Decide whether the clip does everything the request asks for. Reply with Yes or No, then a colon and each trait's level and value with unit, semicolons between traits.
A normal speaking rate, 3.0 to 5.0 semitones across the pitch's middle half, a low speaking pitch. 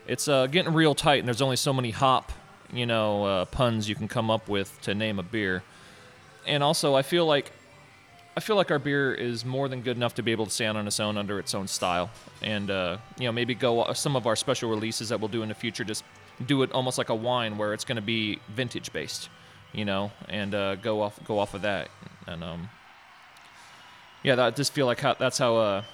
No: fast, 240 wpm; average, 4.2 semitones; low, 115 Hz